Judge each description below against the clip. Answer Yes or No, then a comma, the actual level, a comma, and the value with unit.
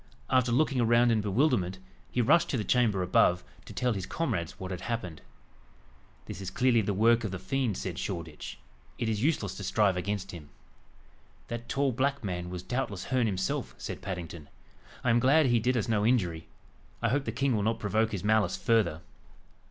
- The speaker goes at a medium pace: Yes, average, 190 wpm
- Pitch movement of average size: Yes, average, 4.8 semitones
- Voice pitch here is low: Yes, low, 110 Hz